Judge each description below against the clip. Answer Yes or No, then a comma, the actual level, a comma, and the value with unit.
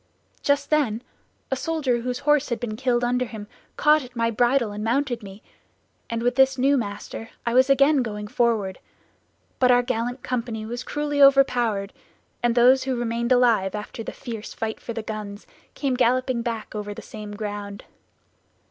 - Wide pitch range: No, average, 3.0 semitones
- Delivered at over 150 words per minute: Yes, average, 175 wpm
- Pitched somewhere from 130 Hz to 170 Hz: No, high, 240 Hz